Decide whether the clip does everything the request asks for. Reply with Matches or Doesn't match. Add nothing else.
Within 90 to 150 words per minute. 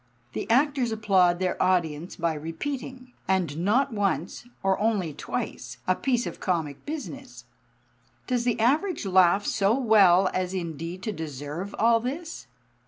Matches